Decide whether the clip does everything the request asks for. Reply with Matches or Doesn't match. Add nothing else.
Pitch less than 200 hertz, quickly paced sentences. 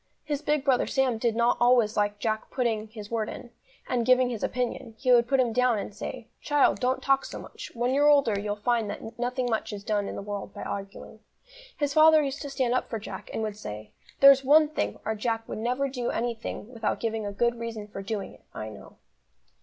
Doesn't match